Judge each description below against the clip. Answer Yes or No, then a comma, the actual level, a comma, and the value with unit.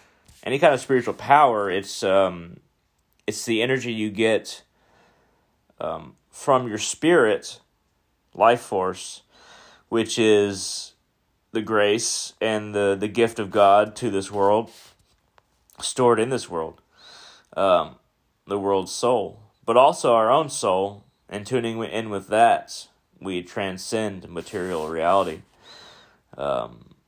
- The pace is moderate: No, slow, 120 wpm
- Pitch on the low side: Yes, low, 105 Hz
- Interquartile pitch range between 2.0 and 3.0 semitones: Yes, narrow, 2.5 semitones